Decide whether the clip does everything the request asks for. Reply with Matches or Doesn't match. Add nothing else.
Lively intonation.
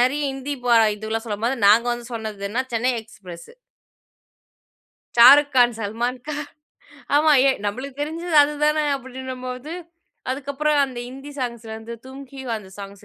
Doesn't match